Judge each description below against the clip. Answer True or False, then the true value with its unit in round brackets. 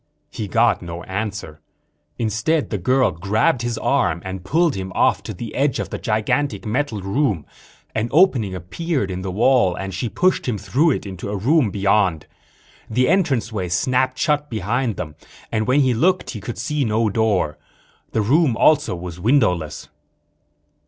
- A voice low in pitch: True (110 Hz)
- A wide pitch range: True (5.9 semitones)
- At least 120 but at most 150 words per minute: False (165 wpm)